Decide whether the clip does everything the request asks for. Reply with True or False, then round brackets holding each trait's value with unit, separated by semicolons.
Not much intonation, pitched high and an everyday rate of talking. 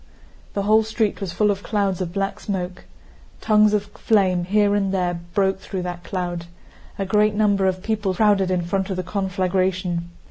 True (2.1 semitones; 195 Hz; 180 wpm)